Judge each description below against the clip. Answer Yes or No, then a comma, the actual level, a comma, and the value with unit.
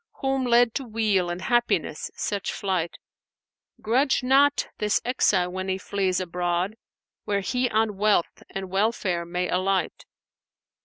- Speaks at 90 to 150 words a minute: Yes, average, 145 wpm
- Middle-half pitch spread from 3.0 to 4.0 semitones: No, average, 4.5 semitones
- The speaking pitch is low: No, high, 200 Hz